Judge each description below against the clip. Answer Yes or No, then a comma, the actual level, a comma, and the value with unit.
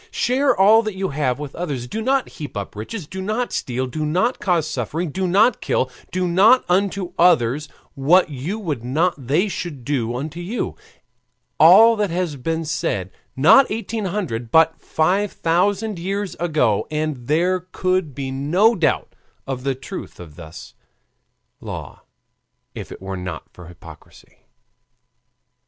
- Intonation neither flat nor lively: No, wide, 6.4 semitones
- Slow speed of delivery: No, average, 155 wpm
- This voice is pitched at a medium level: Yes, medium, 165 Hz